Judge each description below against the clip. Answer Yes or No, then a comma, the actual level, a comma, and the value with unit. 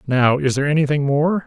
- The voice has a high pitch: No, medium, 145 Hz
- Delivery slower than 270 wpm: Yes, fast, 205 wpm